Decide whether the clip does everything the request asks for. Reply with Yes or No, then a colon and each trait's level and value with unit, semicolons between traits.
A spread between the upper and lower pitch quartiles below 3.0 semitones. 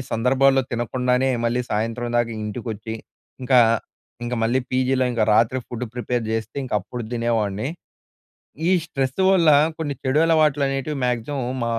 Yes: narrow, 2.5 semitones